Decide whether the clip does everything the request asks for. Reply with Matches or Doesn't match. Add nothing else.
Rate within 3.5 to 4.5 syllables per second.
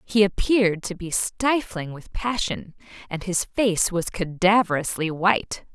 Matches